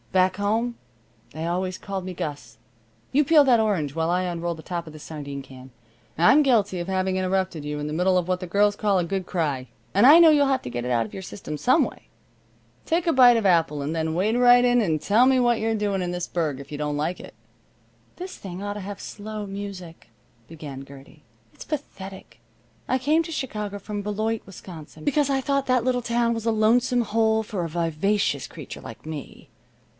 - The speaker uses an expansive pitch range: Yes, wide, 6.1 semitones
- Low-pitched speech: No, high, 195 Hz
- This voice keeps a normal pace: No, fast, 220 wpm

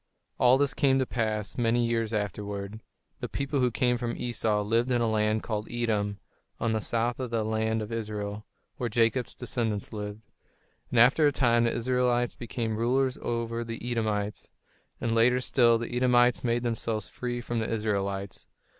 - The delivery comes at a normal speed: Yes, average, 170 wpm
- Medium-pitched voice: No, low, 115 Hz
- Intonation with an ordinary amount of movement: No, narrow, 2.1 semitones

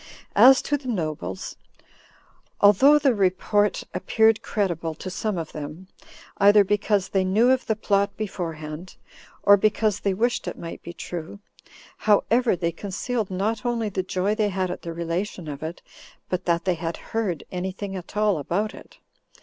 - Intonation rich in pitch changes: No, average, 3.8 semitones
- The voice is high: Yes, high, 195 Hz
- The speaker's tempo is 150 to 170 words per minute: Yes, average, 165 wpm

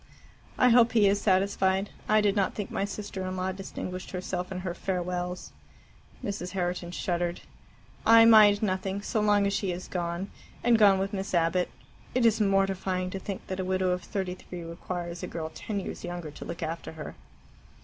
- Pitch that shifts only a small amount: Yes, narrow, 2.0 semitones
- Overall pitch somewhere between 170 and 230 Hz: Yes, high, 190 Hz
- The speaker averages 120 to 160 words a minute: No, average, 190 wpm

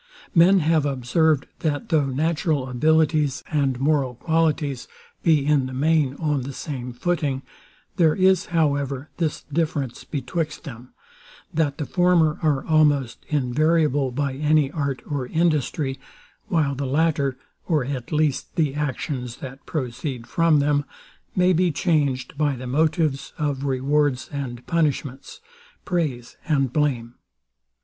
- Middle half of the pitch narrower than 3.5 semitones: Yes, average, 3.0 semitones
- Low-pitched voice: No, medium, 145 Hz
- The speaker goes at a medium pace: No, slow, 130 wpm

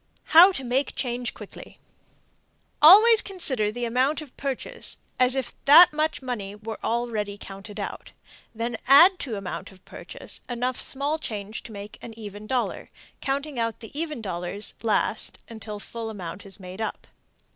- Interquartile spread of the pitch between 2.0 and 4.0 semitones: No, average, 5.0 semitones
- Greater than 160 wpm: No, average, 155 wpm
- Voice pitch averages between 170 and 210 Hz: No, high, 235 Hz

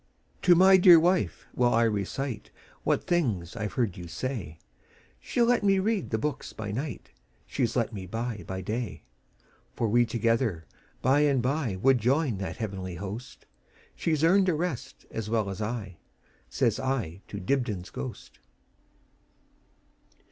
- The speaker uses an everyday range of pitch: No, wide, 6.1 semitones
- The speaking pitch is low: Yes, low, 115 Hz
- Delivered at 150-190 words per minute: No, average, 140 wpm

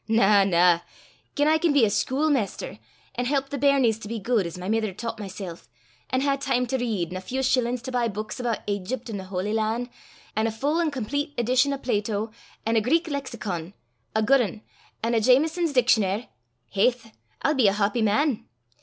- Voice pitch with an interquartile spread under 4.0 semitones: No, average, 4.4 semitones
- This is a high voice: Yes, high, 230 Hz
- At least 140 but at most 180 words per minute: No, average, 200 wpm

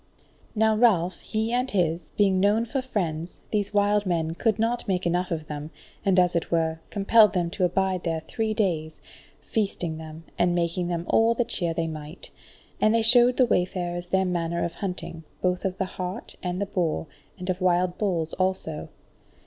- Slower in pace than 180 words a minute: No, average, 185 wpm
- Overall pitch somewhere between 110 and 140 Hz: No, medium, 180 Hz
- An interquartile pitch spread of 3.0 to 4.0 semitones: Yes, average, 3.6 semitones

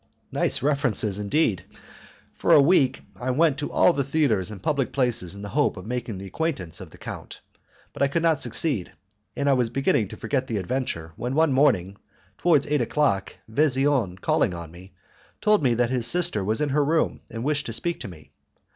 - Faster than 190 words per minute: Yes, average, 200 wpm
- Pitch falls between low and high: No, low, 130 Hz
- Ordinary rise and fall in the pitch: No, wide, 6.3 semitones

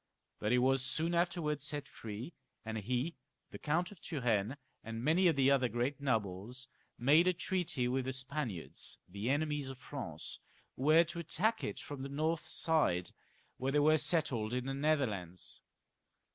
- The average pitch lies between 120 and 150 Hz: Yes, low, 135 Hz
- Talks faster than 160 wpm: Yes, average, 170 wpm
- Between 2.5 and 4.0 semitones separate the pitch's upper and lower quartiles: No, average, 4.4 semitones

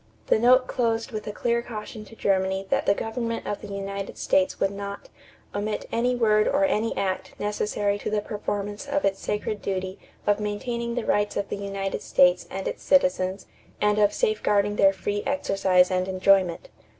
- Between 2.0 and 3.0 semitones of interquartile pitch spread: Yes, average, 2.7 semitones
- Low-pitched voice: No, high, 205 Hz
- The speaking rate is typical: Yes, average, 180 wpm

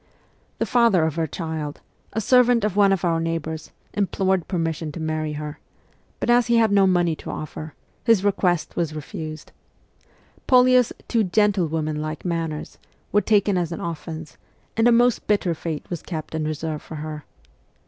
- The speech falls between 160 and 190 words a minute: Yes, average, 175 wpm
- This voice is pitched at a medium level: Yes, medium, 170 Hz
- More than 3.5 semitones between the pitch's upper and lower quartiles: Yes, average, 4.7 semitones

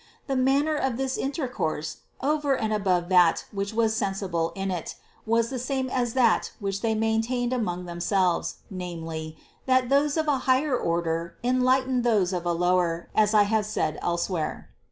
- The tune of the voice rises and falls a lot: Yes, wide, 6.4 semitones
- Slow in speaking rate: No, average, 175 wpm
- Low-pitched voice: No, high, 215 Hz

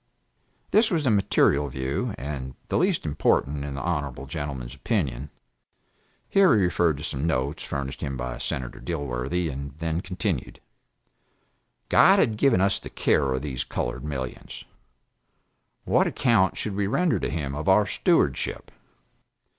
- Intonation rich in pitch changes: Yes, wide, 6.1 semitones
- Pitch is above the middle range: No, very low, 75 Hz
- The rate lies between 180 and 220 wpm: No, average, 145 wpm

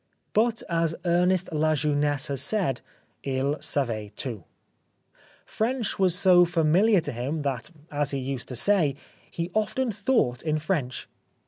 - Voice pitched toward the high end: No, medium, 155 Hz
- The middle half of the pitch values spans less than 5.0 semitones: No, wide, 5.4 semitones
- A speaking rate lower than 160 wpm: Yes, average, 145 wpm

